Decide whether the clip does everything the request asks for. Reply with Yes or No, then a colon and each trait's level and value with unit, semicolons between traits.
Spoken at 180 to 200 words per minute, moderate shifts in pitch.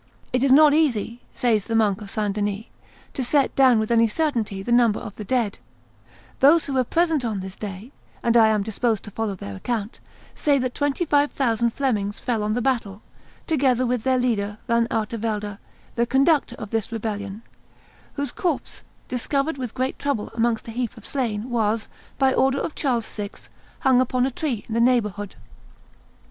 Yes: average, 185 wpm; average, 3.8 semitones